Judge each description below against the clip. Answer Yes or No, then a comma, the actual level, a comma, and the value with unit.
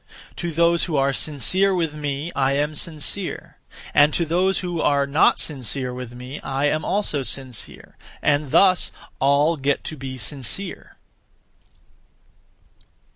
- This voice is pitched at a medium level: Yes, medium, 145 Hz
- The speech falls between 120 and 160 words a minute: Yes, slow, 135 wpm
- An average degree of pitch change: Yes, average, 3.7 semitones